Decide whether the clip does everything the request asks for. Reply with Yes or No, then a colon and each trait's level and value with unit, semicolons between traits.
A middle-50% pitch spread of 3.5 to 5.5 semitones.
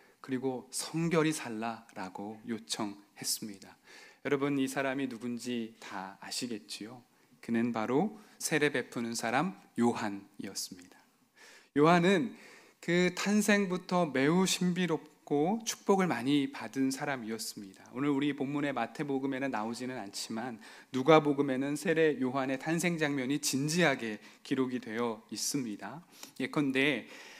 Yes: average, 5.1 semitones